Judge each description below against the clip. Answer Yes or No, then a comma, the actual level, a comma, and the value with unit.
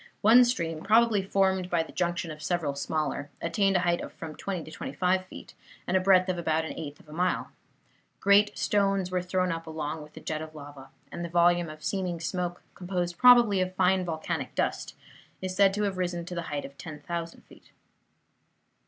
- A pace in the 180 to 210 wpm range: Yes, fast, 205 wpm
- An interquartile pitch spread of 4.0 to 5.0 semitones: No, average, 2.9 semitones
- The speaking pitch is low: No, medium, 175 Hz